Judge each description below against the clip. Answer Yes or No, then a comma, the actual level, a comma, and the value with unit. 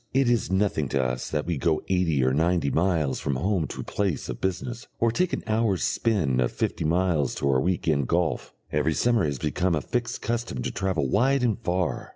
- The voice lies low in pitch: Yes, very low, 90 Hz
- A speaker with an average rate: No, fast, 215 wpm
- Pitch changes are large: Yes, wide, 6.3 semitones